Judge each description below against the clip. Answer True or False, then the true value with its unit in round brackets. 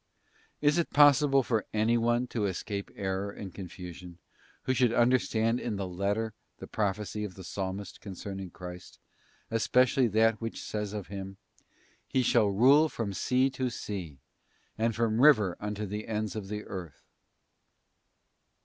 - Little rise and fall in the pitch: False (3.4 semitones)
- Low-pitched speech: True (105 Hz)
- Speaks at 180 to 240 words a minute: False (150 wpm)